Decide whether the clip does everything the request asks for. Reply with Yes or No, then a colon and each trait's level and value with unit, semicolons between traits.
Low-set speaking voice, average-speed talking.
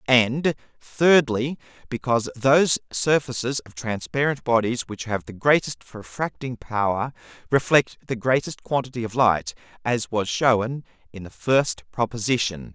No: low, 120 Hz; slow, 125 wpm